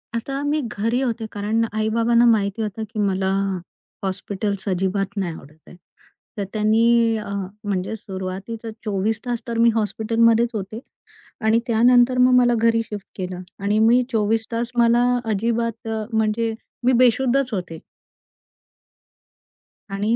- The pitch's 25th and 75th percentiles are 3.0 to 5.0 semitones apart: No, narrow, 2.5 semitones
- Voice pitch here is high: Yes, high, 220 Hz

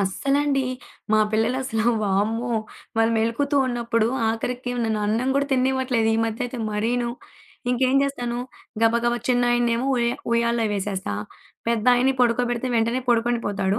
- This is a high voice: Yes, high, 235 Hz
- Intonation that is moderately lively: No, narrow, 1.9 semitones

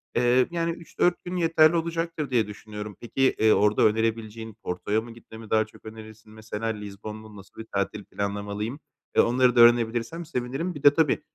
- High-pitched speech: No, low, 115 Hz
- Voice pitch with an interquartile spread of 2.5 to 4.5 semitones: No, average, 4.9 semitones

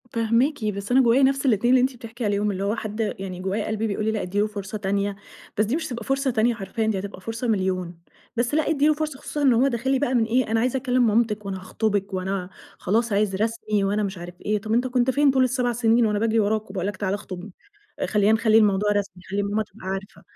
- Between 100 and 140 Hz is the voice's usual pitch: No, high, 220 Hz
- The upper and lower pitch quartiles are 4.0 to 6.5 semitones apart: No, average, 3.4 semitones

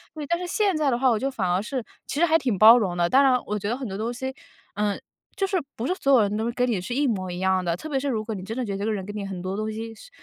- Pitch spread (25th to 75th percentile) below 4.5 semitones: No, average, 5.1 semitones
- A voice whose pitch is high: Yes, high, 225 Hz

